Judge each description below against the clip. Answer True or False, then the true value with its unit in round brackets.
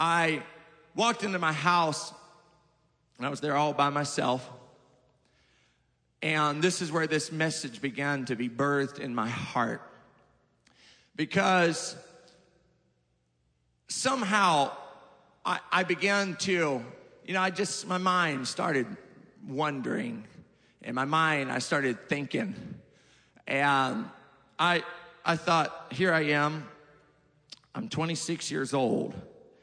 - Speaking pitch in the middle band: True (155 Hz)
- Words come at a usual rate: False (115 wpm)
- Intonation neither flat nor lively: True (3.8 semitones)